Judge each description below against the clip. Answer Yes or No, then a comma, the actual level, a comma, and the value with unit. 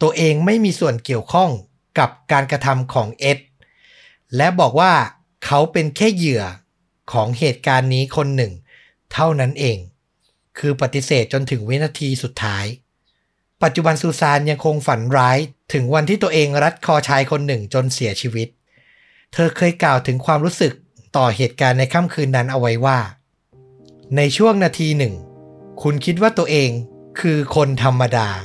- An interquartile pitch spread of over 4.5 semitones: No, average, 4.0 semitones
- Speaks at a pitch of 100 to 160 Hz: Yes, medium, 140 Hz